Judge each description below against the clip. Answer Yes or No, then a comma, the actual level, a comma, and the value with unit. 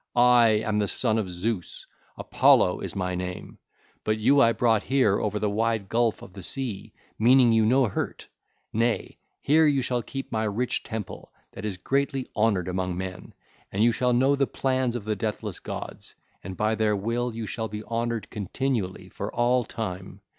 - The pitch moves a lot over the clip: No, average, 3.2 semitones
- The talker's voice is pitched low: Yes, low, 110 Hz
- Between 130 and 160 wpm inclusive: No, average, 180 wpm